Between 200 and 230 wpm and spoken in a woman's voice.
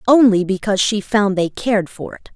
Yes: fast, 205 wpm; female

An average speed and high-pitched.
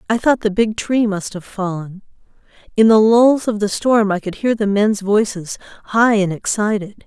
Yes: average, 195 wpm; high, 210 Hz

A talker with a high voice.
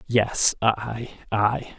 No: low, 110 Hz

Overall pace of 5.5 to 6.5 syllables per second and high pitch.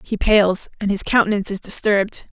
Yes: 5.7 syllables/s; high, 205 Hz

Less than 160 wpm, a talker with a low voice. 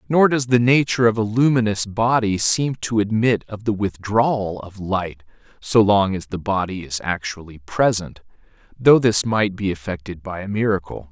No: average, 175 wpm; low, 105 Hz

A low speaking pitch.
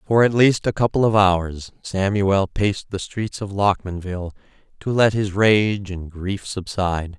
Yes: low, 100 Hz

